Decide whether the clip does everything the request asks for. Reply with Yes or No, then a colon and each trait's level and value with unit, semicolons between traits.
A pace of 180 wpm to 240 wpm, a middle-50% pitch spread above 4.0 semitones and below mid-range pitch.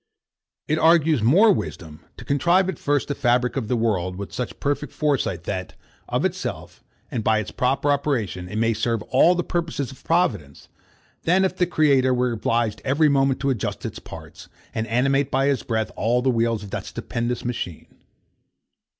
Yes: average, 185 wpm; average, 4.4 semitones; low, 130 Hz